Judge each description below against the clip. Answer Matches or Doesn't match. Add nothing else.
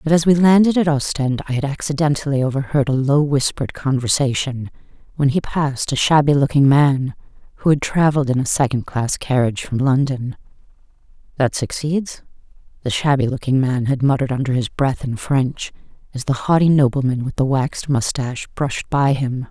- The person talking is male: Doesn't match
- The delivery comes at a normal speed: Matches